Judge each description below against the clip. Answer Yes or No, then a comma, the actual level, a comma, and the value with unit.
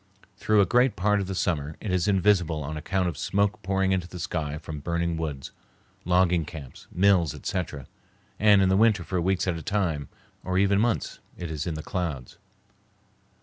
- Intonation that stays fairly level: No, average, 3.6 semitones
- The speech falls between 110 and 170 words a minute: No, average, 185 wpm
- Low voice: Yes, very low, 90 Hz